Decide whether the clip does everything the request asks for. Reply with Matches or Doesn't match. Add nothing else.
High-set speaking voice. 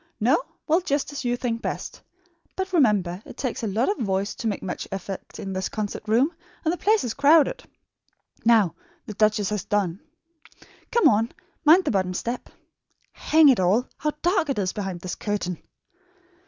Matches